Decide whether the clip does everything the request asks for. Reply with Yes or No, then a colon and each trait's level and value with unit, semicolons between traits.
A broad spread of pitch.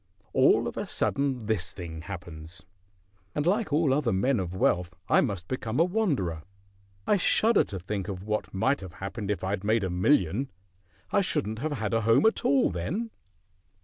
Yes: wide, 7.2 semitones